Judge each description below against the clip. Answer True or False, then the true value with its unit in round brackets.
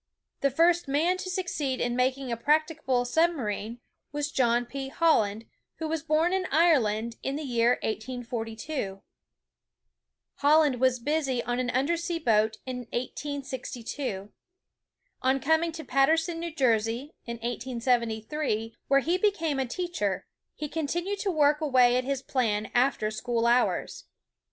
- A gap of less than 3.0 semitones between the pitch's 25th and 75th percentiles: False (4.9 semitones)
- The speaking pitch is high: True (265 Hz)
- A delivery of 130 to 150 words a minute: True (145 wpm)